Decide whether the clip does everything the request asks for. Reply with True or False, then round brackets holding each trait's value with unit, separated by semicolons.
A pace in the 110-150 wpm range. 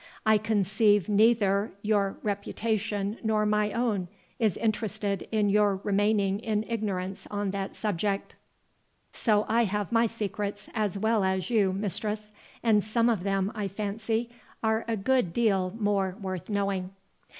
True (140 wpm)